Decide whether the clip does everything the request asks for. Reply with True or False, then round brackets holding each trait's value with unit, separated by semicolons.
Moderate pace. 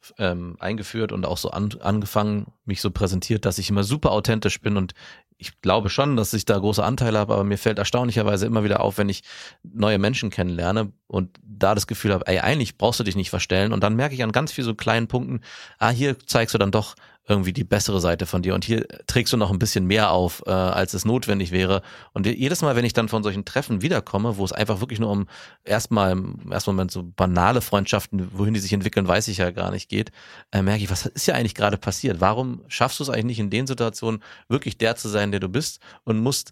False (240 wpm)